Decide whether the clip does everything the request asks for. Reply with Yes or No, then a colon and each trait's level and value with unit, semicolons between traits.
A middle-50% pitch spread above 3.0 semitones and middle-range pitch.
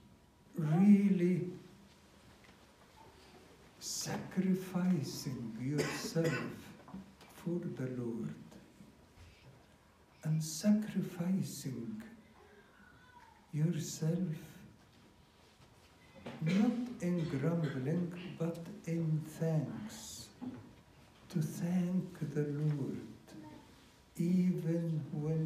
Yes: average, 4.8 semitones; medium, 165 Hz